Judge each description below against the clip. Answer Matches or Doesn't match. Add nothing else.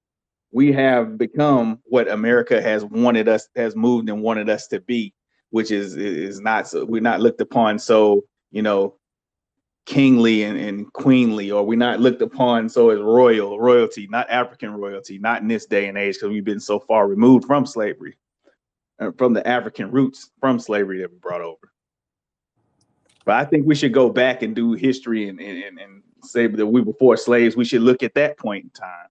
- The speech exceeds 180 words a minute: Matches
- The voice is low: Matches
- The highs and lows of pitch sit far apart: Doesn't match